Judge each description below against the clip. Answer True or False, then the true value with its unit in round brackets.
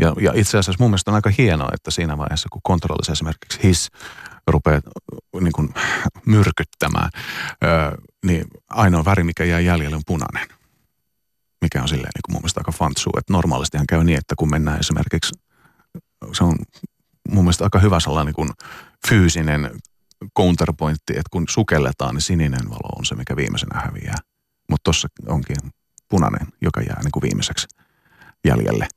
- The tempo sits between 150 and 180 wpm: True (155 wpm)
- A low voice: True (80 Hz)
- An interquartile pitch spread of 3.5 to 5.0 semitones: True (3.9 semitones)